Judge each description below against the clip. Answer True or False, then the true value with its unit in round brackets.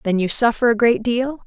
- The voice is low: False (235 Hz)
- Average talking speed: False (245 wpm)